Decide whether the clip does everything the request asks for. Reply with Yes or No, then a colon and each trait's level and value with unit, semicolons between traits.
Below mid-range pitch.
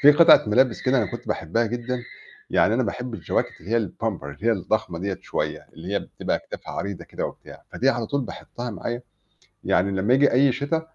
Yes: low, 115 Hz